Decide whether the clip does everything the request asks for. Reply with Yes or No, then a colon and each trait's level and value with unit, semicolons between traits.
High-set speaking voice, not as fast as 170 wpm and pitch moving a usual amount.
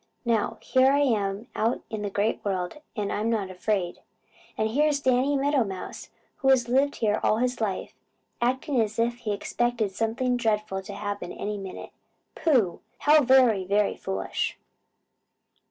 Yes: high, 225 Hz; average, 155 wpm; average, 4.0 semitones